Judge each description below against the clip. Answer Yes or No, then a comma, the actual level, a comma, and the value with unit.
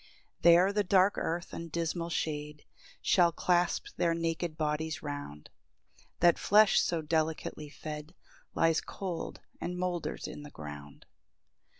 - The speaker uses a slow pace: Yes, slow, 130 wpm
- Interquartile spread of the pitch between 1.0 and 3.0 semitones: Yes, narrow, 2.6 semitones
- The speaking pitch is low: No, medium, 165 Hz